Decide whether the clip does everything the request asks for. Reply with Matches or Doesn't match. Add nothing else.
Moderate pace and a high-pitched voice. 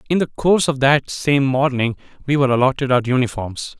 Doesn't match